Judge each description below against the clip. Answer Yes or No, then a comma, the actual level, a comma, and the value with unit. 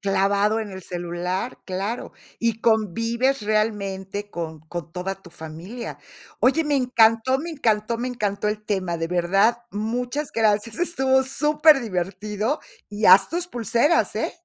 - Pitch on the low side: No, high, 215 Hz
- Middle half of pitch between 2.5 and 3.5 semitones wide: No, average, 4.3 semitones